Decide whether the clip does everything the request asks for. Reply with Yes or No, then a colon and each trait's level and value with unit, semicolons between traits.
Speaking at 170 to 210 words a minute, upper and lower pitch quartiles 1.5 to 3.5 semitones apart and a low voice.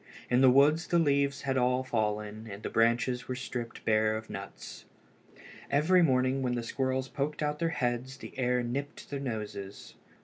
Yes: average, 175 wpm; average, 3.0 semitones; low, 130 Hz